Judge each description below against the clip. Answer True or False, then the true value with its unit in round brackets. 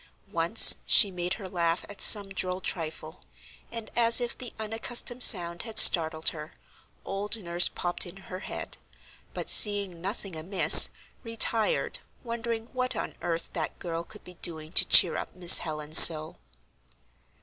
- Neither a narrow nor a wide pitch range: True (4.6 semitones)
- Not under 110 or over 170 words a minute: True (150 wpm)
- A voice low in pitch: False (185 Hz)